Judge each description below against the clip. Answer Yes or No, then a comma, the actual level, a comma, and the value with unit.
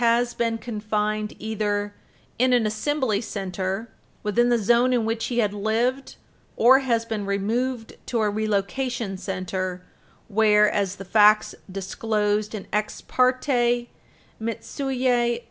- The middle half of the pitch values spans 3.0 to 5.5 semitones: No, narrow, 2.6 semitones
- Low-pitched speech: No, high, 220 Hz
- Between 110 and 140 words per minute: Yes, slow, 135 wpm